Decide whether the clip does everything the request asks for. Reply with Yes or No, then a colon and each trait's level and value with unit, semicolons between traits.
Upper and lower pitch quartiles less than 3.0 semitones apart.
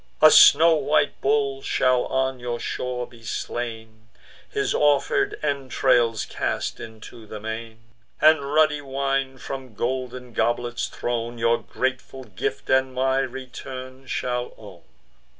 Yes: narrow, 2.5 semitones